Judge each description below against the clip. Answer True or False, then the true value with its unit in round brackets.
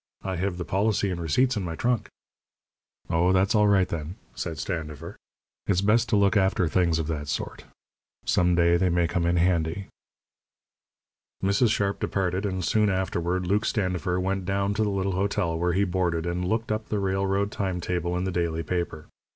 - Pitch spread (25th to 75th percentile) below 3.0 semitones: True (2.5 semitones)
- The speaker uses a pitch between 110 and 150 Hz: False (95 Hz)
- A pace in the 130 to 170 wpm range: False (185 wpm)